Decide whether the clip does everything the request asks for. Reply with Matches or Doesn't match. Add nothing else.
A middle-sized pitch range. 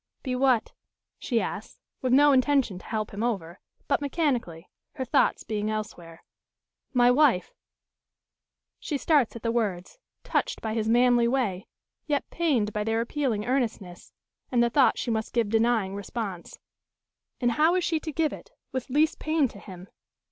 Matches